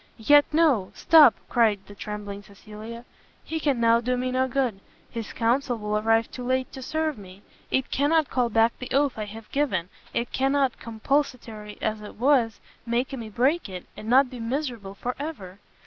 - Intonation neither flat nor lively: Yes, average, 4.0 semitones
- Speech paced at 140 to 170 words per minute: No, average, 185 wpm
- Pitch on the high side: Yes, high, 235 Hz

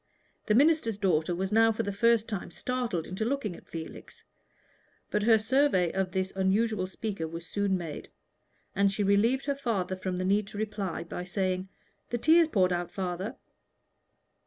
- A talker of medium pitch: No, high, 200 Hz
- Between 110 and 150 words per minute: No, average, 175 wpm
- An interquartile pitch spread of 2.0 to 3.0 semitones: No, average, 3.5 semitones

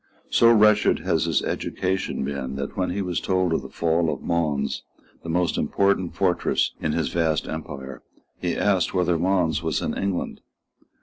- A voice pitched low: Yes, very low, 85 Hz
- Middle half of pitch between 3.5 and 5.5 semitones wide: No, average, 3.0 semitones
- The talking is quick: No, average, 170 wpm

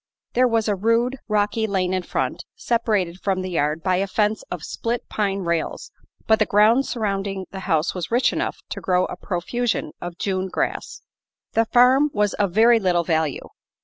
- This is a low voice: No, high, 200 Hz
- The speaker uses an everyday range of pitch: Yes, average, 3.8 semitones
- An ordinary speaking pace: Yes, average, 180 wpm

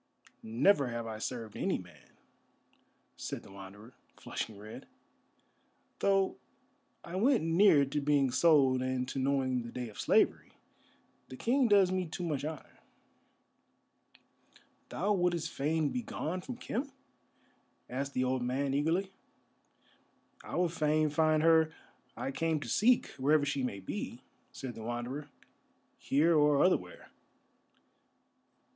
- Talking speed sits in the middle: No, slow, 130 wpm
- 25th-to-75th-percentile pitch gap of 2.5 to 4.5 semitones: No, average, 4.9 semitones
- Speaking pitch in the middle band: Yes, medium, 145 Hz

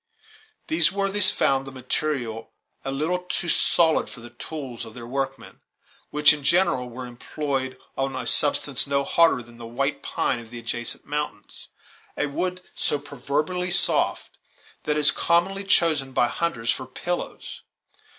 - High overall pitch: No, medium, 140 Hz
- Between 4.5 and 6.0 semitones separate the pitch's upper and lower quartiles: Yes, average, 5.1 semitones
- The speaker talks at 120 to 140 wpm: No, average, 160 wpm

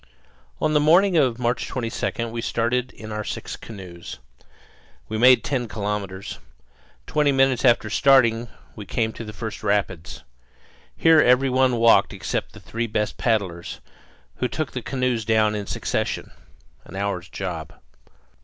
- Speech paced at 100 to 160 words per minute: Yes, average, 145 wpm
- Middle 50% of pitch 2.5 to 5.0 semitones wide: Yes, average, 3.6 semitones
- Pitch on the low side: Yes, low, 115 Hz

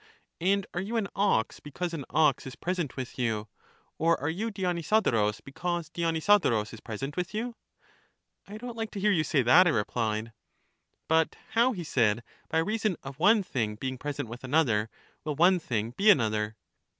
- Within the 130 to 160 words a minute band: No, average, 180 wpm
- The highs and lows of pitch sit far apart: Yes, wide, 7.8 semitones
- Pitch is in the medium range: Yes, medium, 160 Hz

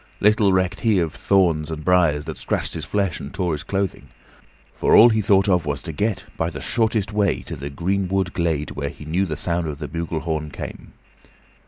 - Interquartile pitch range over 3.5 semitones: Yes, average, 4.1 semitones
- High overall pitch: No, very low, 90 Hz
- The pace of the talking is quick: Yes, fast, 210 wpm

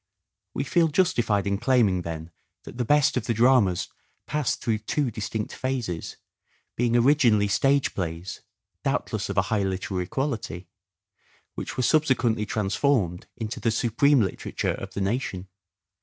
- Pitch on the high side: No, low, 115 Hz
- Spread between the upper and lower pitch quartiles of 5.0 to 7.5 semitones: Yes, average, 5.3 semitones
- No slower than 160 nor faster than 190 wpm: No, average, 150 wpm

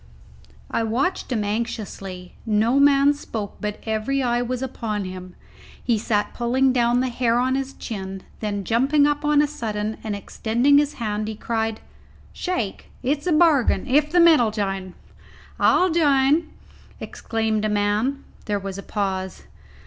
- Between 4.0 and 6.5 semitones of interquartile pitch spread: Yes, average, 4.7 semitones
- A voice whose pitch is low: No, high, 235 Hz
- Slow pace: No, average, 155 wpm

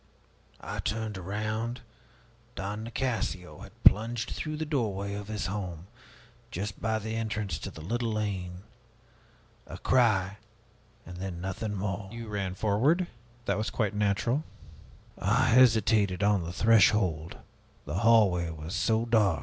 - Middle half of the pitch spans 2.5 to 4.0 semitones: Yes, average, 2.9 semitones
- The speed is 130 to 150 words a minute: Yes, slow, 135 wpm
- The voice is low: Yes, low, 105 Hz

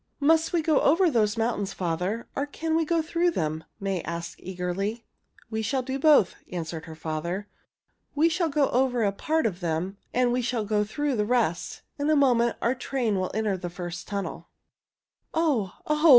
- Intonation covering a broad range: Yes, wide, 7.6 semitones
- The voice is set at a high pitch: Yes, high, 225 Hz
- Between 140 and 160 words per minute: No, average, 185 wpm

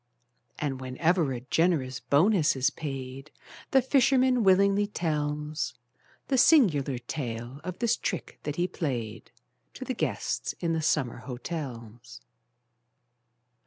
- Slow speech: Yes, slow, 120 wpm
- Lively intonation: Yes, wide, 6.0 semitones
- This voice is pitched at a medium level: Yes, medium, 150 Hz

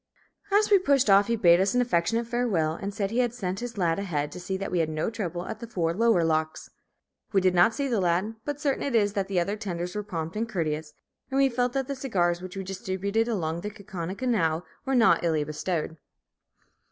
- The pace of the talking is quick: Yes, fast, 230 wpm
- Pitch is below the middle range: No, high, 195 Hz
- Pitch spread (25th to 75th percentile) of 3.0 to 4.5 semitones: No, average, 5.2 semitones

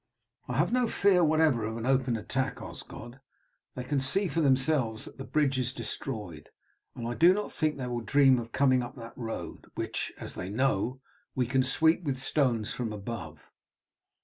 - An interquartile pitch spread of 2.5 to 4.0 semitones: Yes, average, 3.7 semitones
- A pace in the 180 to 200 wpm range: Yes, average, 185 wpm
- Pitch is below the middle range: Yes, low, 130 Hz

